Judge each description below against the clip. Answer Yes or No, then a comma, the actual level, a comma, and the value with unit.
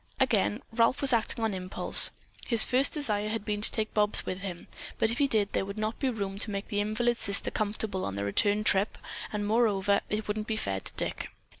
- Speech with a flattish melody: Yes, narrow, 2.0 semitones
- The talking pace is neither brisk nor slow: No, fast, 220 wpm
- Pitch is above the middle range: Yes, high, 210 Hz